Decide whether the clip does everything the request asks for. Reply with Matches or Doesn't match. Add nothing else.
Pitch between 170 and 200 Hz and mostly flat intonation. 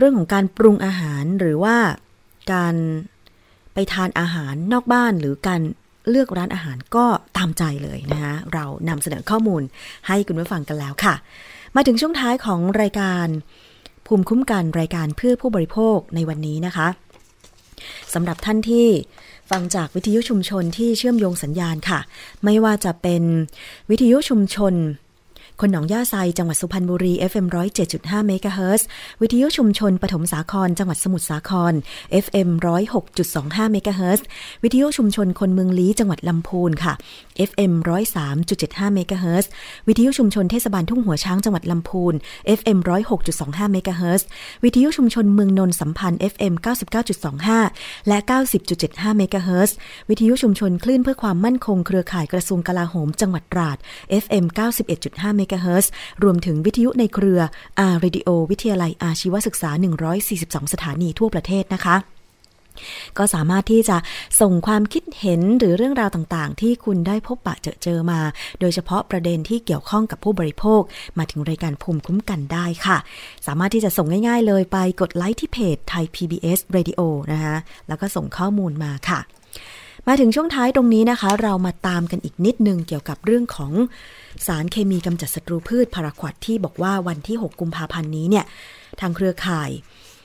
Doesn't match